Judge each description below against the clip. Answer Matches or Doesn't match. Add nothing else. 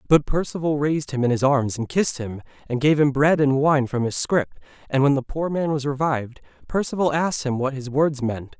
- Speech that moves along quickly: Matches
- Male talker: Matches